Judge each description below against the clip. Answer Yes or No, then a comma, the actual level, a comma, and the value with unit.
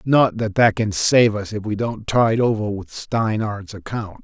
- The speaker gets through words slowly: No, average, 200 wpm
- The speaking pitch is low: Yes, low, 105 Hz